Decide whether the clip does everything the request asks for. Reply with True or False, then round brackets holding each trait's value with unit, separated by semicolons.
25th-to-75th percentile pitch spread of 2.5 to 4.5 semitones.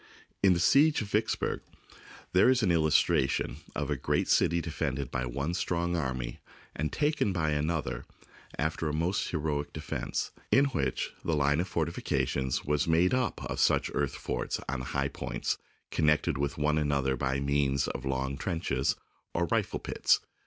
True (3.9 semitones)